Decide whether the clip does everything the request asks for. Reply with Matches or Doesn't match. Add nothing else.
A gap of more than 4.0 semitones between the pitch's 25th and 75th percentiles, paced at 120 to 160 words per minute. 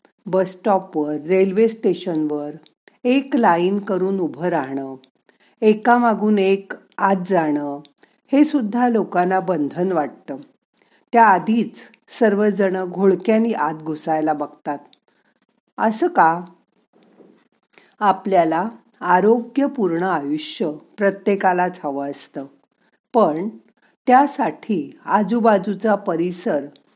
Doesn't match